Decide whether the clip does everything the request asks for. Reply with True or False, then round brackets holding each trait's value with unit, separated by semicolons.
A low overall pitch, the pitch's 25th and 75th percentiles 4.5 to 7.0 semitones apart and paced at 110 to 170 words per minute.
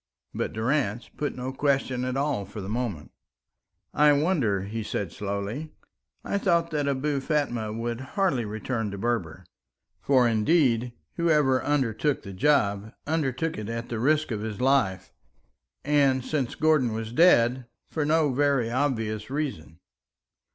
True (125 Hz; 5.0 semitones; 145 wpm)